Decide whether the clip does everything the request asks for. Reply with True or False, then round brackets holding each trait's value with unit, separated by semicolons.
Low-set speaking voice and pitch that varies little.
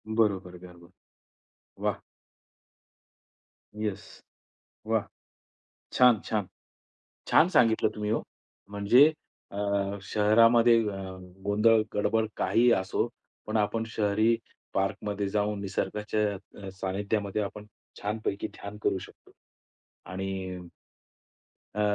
True (105 Hz; 2.0 semitones)